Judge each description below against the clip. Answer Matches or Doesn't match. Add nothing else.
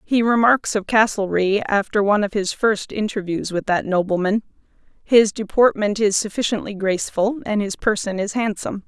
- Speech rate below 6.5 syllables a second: Matches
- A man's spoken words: Doesn't match